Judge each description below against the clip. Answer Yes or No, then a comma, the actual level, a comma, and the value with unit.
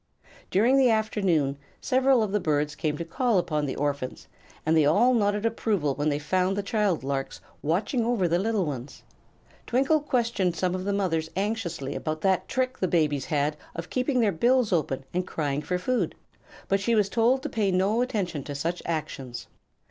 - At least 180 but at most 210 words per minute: Yes, average, 185 wpm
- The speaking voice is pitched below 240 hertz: Yes, medium, 185 Hz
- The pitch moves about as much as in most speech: No, wide, 6.6 semitones